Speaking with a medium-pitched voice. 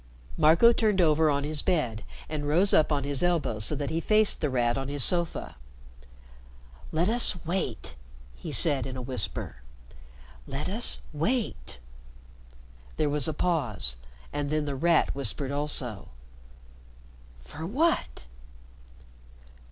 Yes: medium, 150 Hz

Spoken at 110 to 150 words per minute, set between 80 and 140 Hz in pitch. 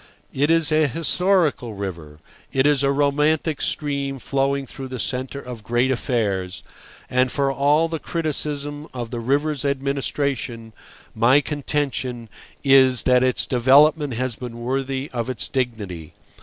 Yes: average, 140 wpm; low, 135 Hz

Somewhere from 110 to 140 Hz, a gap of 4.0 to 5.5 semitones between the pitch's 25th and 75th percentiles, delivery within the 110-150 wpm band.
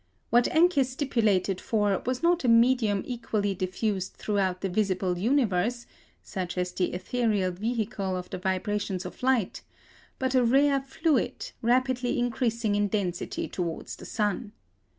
No: high, 215 Hz; average, 4.7 semitones; average, 140 wpm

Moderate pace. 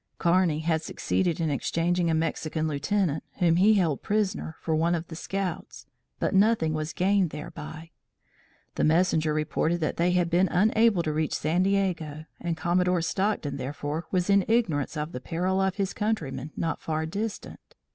Yes: average, 165 wpm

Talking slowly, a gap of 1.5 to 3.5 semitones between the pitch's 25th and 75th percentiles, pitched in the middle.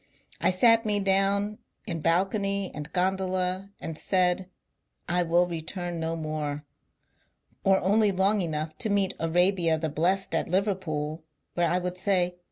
No: average, 150 wpm; average, 2.9 semitones; medium, 180 Hz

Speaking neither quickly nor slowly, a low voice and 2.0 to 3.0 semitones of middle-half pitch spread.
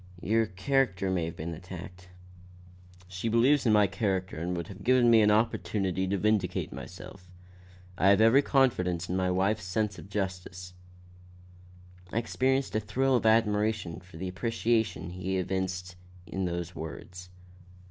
No: average, 150 wpm; very low, 95 Hz; average, 3.5 semitones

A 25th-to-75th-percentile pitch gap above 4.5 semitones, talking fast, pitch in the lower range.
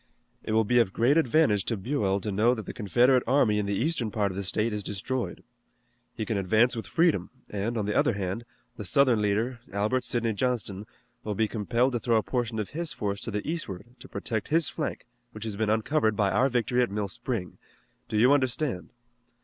No: average, 3.3 semitones; fast, 215 wpm; low, 110 Hz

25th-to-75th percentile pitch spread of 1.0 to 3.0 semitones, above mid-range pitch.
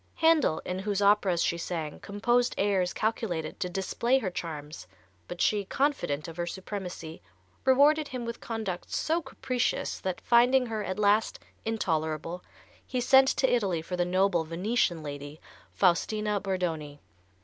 No: wide, 5.4 semitones; high, 195 Hz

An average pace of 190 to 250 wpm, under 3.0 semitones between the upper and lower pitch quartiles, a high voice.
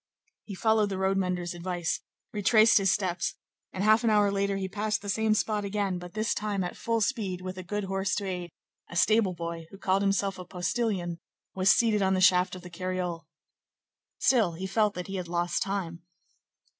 Yes: average, 200 wpm; narrow, 2.6 semitones; high, 195 Hz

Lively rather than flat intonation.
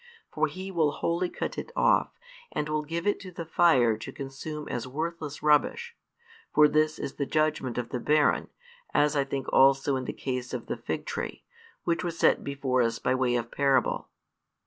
No: average, 3.8 semitones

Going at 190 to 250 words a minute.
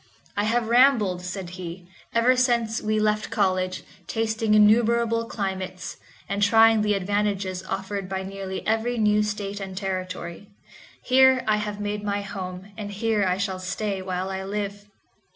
No: average, 150 wpm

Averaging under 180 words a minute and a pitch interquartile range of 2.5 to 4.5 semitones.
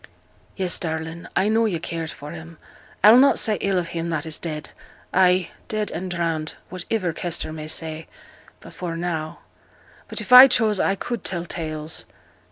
Yes: average, 170 wpm; average, 3.2 semitones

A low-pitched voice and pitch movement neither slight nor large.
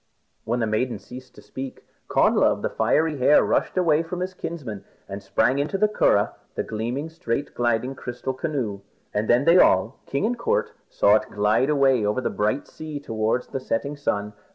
No: low, 130 Hz; wide, 5.8 semitones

